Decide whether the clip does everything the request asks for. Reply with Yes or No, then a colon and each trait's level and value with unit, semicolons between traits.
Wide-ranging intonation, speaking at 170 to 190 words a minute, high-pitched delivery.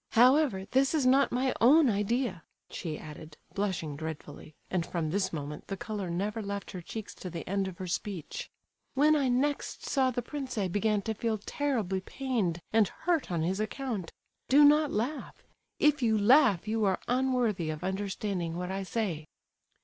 Yes: wide, 6.2 semitones; average, 175 wpm; high, 205 Hz